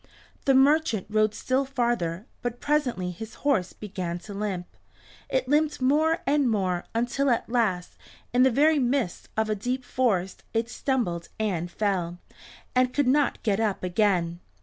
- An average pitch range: No, wide, 5.8 semitones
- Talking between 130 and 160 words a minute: Yes, average, 155 wpm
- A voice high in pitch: Yes, high, 230 Hz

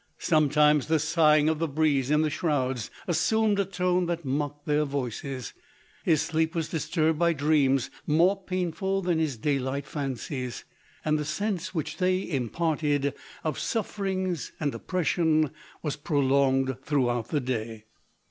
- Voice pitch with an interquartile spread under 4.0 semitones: Yes, average, 3.6 semitones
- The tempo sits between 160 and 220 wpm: No, average, 150 wpm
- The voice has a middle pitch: Yes, medium, 150 Hz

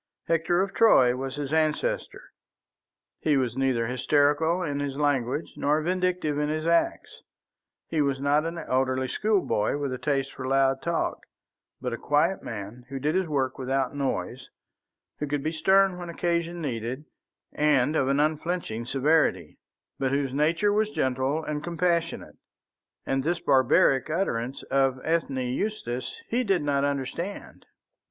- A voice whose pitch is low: No, medium, 145 Hz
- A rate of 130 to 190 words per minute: Yes, average, 150 wpm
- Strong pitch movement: No, average, 4.1 semitones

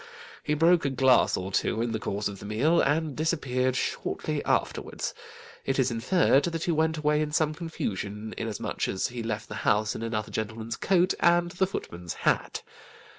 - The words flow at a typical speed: Yes, average, 180 wpm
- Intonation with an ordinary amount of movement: No, wide, 6.6 semitones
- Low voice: Yes, low, 130 Hz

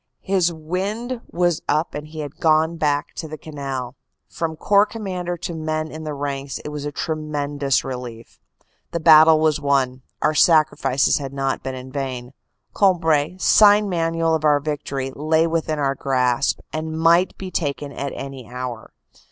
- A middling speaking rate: Yes, average, 170 wpm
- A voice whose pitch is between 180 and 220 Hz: No, medium, 155 Hz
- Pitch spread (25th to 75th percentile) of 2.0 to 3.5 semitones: Yes, average, 3.1 semitones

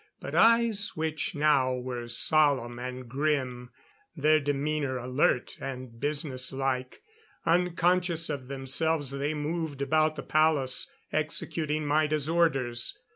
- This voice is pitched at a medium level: Yes, medium, 145 Hz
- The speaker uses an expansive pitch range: No, average, 3.2 semitones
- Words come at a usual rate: No, slow, 115 wpm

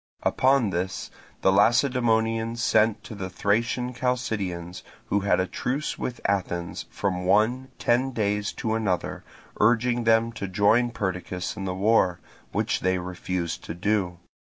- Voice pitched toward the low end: Yes, low, 105 Hz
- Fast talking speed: No, average, 140 wpm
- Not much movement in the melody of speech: No, average, 4.0 semitones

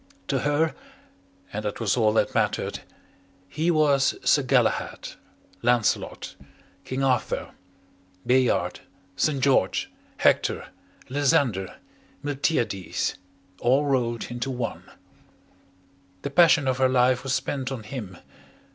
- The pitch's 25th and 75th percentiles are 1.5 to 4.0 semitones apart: Yes, average, 3.1 semitones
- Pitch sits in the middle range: No, low, 130 Hz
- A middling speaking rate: No, slow, 110 wpm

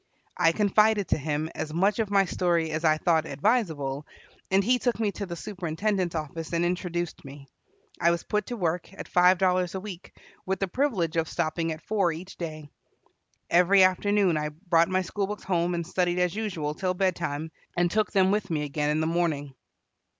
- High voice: No, medium, 175 Hz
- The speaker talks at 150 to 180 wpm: No, average, 200 wpm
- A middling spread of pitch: Yes, average, 3.4 semitones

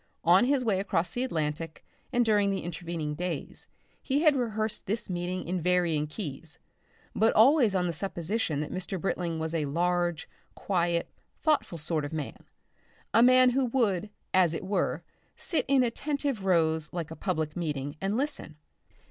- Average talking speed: Yes, average, 165 wpm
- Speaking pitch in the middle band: Yes, medium, 180 Hz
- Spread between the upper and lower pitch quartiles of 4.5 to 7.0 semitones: Yes, wide, 5.5 semitones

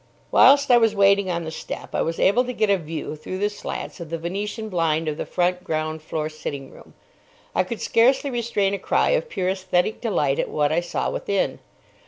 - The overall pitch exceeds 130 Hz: Yes, medium, 185 Hz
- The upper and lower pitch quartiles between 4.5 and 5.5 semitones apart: Yes, average, 5.2 semitones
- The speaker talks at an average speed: No, fast, 215 wpm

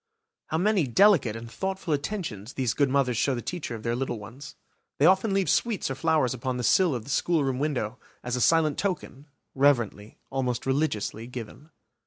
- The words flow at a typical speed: Yes, average, 185 wpm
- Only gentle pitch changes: No, average, 5.2 semitones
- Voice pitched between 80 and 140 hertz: Yes, low, 135 Hz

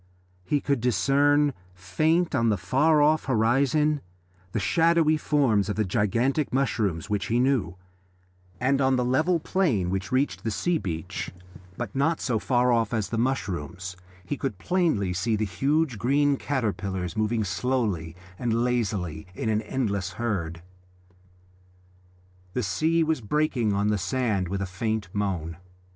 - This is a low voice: Yes, low, 115 Hz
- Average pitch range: No, wide, 6.0 semitones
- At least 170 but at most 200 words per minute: No, average, 150 wpm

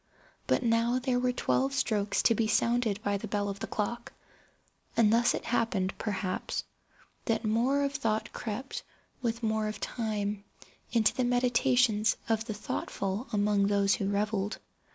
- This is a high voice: Yes, high, 220 Hz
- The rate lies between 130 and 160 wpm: Yes, average, 155 wpm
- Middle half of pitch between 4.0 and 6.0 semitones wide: No, average, 2.8 semitones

